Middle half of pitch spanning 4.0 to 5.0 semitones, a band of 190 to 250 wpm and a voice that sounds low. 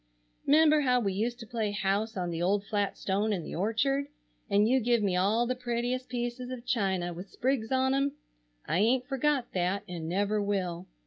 No: average, 4.5 semitones; average, 195 wpm; high, 220 Hz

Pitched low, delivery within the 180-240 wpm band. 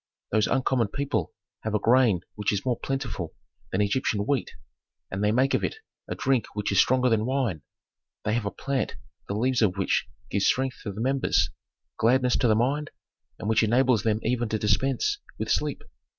Yes: low, 115 Hz; average, 190 wpm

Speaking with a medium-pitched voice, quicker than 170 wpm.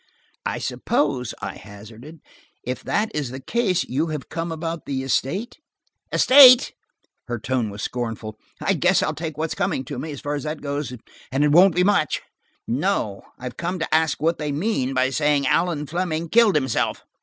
Yes: medium, 150 Hz; average, 180 wpm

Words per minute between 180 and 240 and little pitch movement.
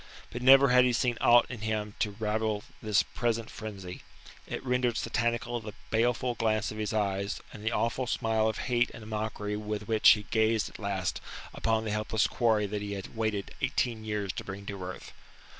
Yes: average, 190 wpm; narrow, 2.0 semitones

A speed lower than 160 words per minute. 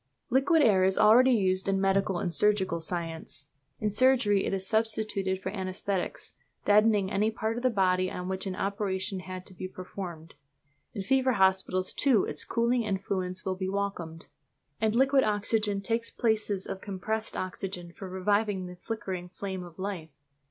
No: average, 165 wpm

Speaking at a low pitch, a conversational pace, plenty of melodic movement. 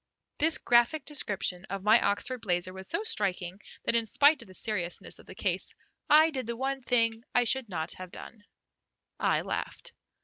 No: high, 230 Hz; average, 180 wpm; wide, 5.8 semitones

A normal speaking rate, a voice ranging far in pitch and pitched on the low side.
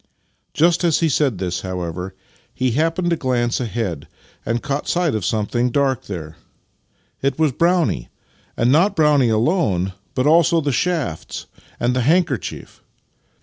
Yes: average, 145 wpm; wide, 6.9 semitones; low, 130 Hz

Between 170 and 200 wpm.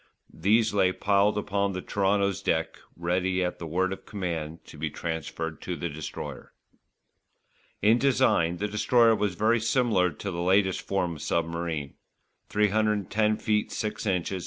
No: average, 150 wpm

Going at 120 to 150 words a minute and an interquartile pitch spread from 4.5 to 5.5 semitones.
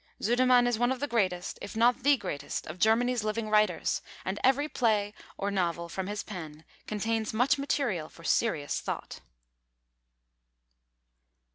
Yes: average, 145 wpm; average, 4.8 semitones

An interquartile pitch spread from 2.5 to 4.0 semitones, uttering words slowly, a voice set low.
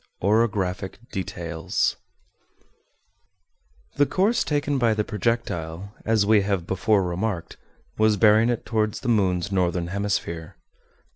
Yes: average, 3.7 semitones; slow, 115 wpm; low, 105 Hz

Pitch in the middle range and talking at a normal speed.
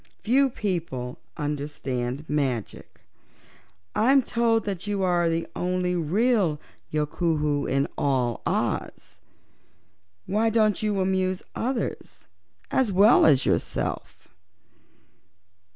No: medium, 180 Hz; slow, 95 wpm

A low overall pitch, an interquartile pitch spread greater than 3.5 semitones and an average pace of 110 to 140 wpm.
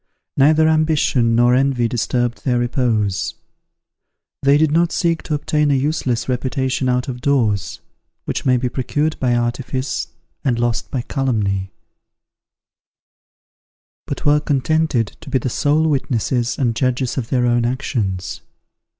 No: low, 130 Hz; average, 3.2 semitones; slow, 135 wpm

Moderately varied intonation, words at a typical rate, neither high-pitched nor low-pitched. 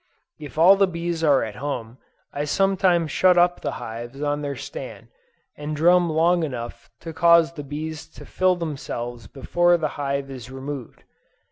Yes: average, 3.9 semitones; average, 165 wpm; medium, 155 Hz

